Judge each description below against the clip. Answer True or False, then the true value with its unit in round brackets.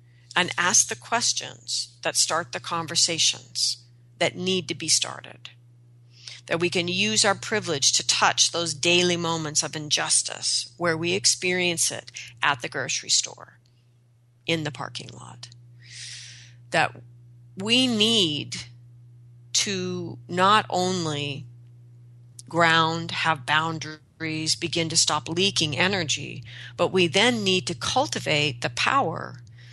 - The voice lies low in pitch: False (150 Hz)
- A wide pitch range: True (6.2 semitones)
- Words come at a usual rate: False (120 wpm)